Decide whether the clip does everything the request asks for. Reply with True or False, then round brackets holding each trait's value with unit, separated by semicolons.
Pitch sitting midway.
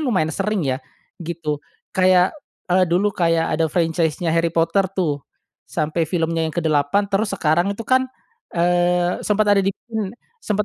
True (175 Hz)